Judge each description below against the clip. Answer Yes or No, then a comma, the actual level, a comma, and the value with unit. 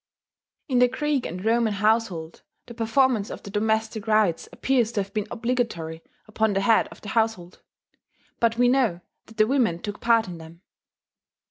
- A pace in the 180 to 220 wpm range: No, average, 170 wpm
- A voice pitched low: No, high, 220 Hz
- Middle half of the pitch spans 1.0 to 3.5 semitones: Yes, average, 3.1 semitones